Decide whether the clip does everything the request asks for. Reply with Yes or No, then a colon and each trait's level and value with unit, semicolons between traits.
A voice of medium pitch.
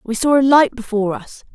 No: high, 245 Hz